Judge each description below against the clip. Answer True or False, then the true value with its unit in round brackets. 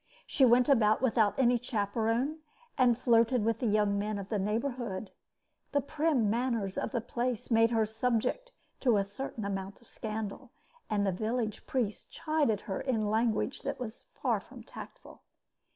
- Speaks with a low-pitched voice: False (225 Hz)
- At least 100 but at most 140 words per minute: False (165 wpm)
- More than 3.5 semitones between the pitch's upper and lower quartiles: False (3.0 semitones)